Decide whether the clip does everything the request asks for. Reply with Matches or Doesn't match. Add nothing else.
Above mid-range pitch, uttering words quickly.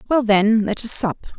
Matches